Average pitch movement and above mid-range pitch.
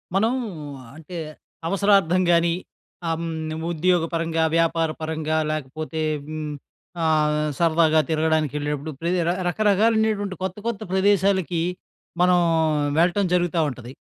No: average, 3.1 semitones; medium, 165 Hz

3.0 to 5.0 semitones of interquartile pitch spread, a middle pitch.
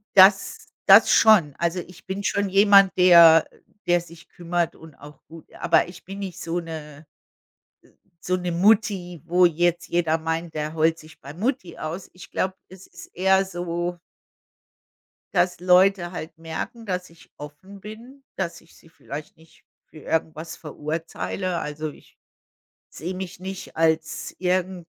No: narrow, 2.6 semitones; medium, 175 Hz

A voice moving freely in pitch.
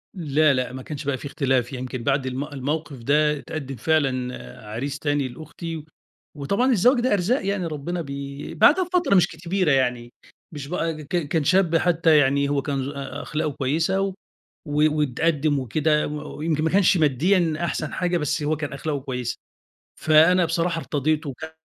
No: average, 3.3 semitones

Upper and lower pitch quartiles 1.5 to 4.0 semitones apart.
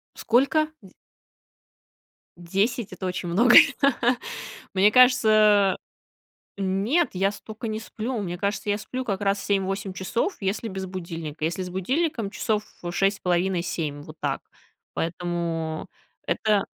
Yes: average, 3.3 semitones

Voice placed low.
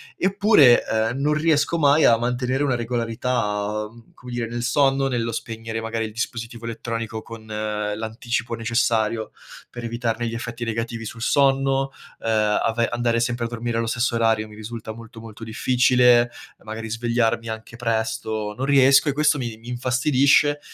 Yes: low, 115 Hz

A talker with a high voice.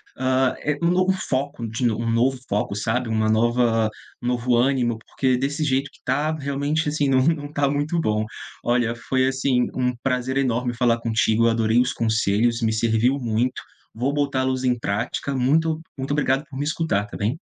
No: low, 125 Hz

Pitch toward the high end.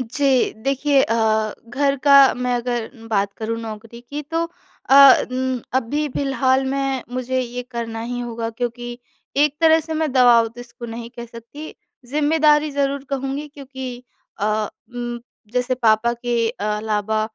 Yes: very high, 250 Hz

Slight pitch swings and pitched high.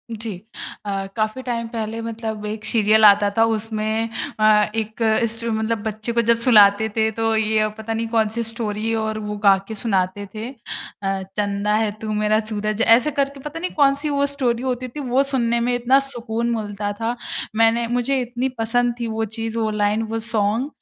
Yes: narrow, 1.8 semitones; high, 225 Hz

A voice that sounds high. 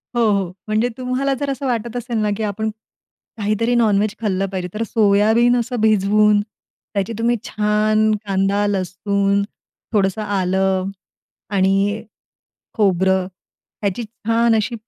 Yes: high, 210 Hz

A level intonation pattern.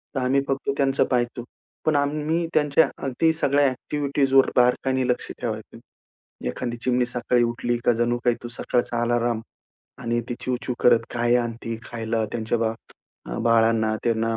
Yes: narrow, 2.3 semitones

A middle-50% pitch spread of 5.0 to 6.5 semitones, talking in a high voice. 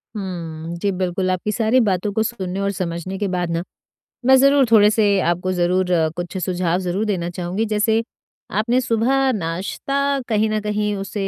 No: average, 3.4 semitones; high, 195 Hz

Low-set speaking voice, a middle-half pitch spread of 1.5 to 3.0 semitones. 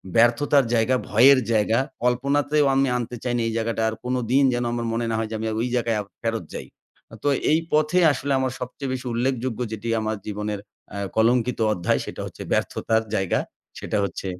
Yes: low, 120 Hz; average, 2.7 semitones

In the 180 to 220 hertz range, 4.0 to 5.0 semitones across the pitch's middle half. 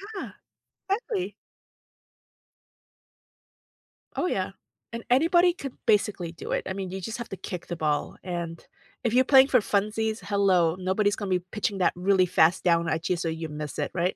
Yes: high, 190 Hz; average, 4.7 semitones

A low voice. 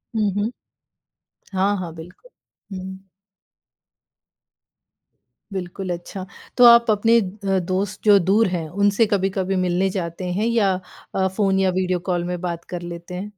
No: high, 190 Hz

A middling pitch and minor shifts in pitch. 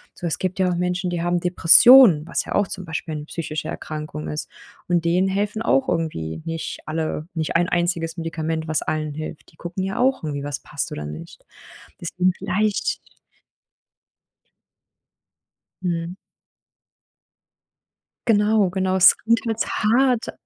No: medium, 175 Hz; average, 3.3 semitones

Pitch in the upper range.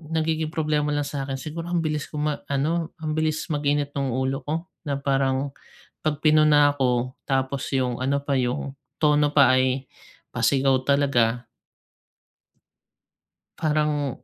No: medium, 145 Hz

